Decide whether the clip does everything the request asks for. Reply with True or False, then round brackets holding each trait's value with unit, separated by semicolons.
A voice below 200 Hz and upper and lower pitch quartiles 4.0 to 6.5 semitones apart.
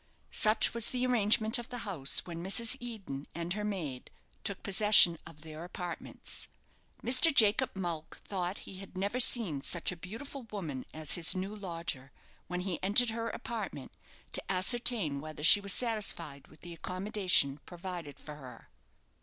True (185 Hz; 4.8 semitones)